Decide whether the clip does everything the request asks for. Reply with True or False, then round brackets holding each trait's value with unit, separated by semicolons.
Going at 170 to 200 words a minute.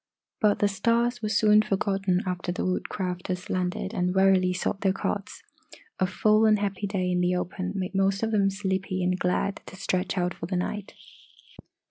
True (180 wpm)